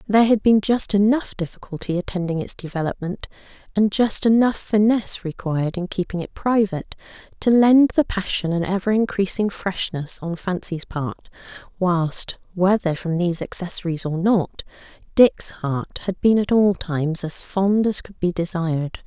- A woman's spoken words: Yes, female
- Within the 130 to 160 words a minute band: Yes, average, 155 wpm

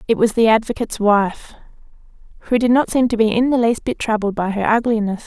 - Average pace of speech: No, fast, 215 wpm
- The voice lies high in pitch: Yes, high, 220 Hz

